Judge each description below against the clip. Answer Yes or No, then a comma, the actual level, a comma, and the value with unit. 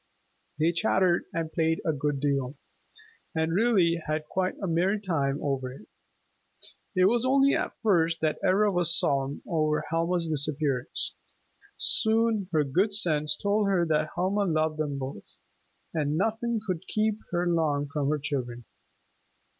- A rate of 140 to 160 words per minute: Yes, average, 145 wpm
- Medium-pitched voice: Yes, medium, 165 Hz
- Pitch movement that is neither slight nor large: Yes, average, 4.5 semitones